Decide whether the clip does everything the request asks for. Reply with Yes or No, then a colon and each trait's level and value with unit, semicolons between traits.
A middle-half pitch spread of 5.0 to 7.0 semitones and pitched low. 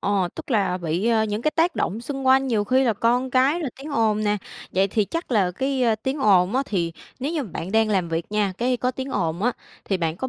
No: average, 5.3 semitones; high, 225 Hz